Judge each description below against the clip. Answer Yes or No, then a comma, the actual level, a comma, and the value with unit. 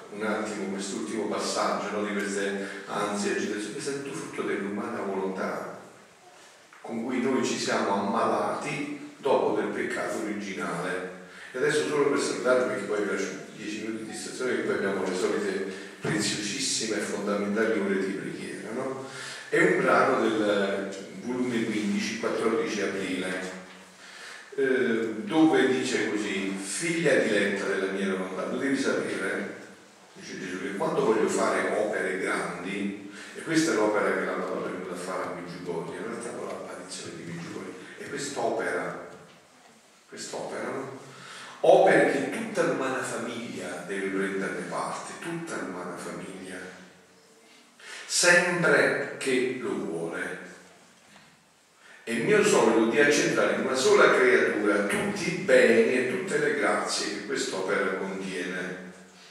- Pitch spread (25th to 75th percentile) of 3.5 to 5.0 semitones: No, average, 3.1 semitones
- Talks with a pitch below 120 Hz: Yes, low, 100 Hz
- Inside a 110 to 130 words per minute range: No, average, 140 wpm